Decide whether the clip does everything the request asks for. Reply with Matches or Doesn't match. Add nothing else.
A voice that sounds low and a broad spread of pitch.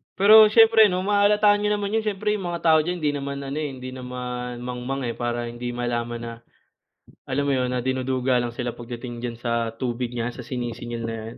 Matches